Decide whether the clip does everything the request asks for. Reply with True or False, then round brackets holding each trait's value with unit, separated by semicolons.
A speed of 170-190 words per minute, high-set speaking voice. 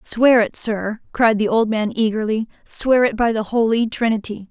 True (175 wpm; 220 Hz)